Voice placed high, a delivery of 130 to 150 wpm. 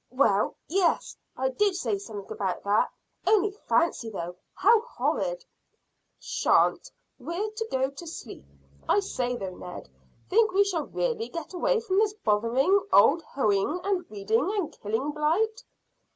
Yes: very high, 325 Hz; average, 145 wpm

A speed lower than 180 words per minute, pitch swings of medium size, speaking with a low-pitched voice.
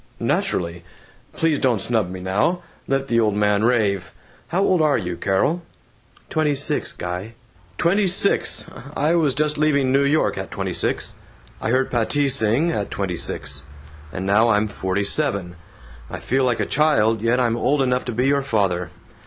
No: average, 170 wpm; wide, 6.3 semitones; low, 120 Hz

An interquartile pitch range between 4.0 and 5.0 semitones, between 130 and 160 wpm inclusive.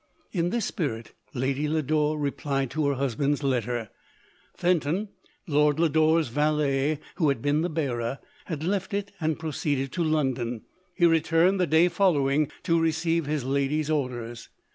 No: average, 3.1 semitones; average, 145 wpm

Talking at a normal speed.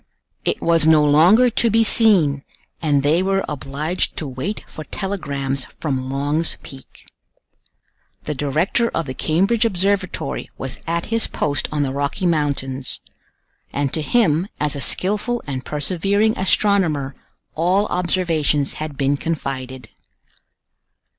No: slow, 130 wpm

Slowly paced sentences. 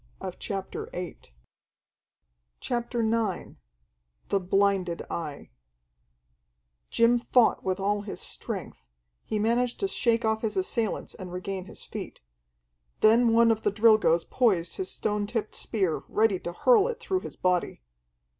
Yes: slow, 125 wpm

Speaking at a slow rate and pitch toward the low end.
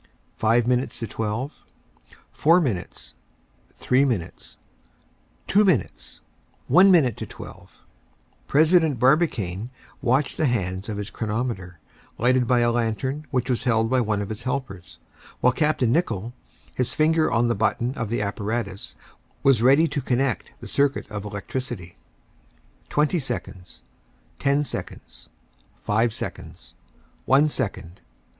Yes: slow, 130 wpm; low, 120 Hz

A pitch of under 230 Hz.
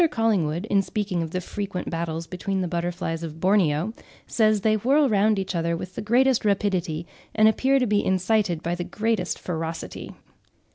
Yes: high, 190 Hz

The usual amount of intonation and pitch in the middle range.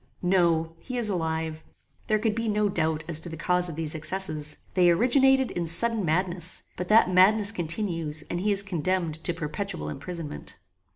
Yes: average, 4.0 semitones; medium, 180 Hz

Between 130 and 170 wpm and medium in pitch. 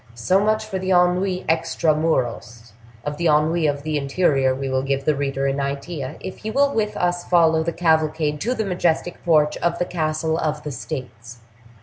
No: average, 195 wpm; medium, 155 Hz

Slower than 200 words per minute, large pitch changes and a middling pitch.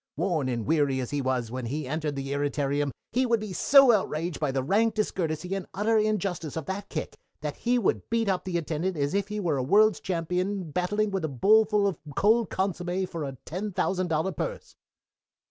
No: fast, 205 wpm; wide, 5.7 semitones; medium, 180 Hz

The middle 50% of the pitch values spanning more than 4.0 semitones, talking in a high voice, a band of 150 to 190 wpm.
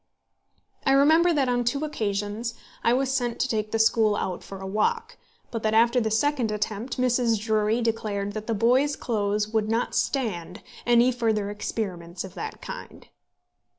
No: average, 3.2 semitones; high, 225 Hz; average, 170 wpm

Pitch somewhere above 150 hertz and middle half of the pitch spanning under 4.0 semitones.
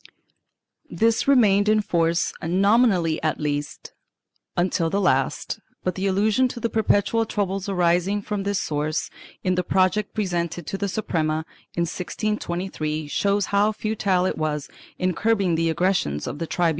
Yes: medium, 185 Hz; average, 3.6 semitones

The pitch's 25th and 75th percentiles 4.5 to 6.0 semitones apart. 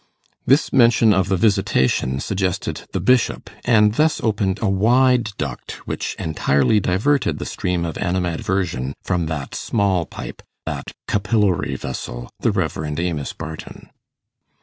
Yes: wide, 5.4 semitones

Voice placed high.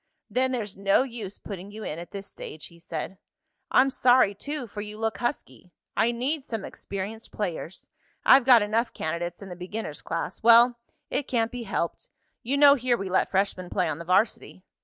Yes: high, 210 Hz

